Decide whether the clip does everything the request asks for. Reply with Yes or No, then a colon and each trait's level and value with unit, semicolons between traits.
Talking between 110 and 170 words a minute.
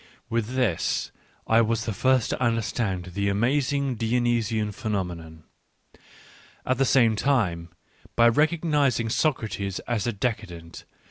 Yes: average, 150 wpm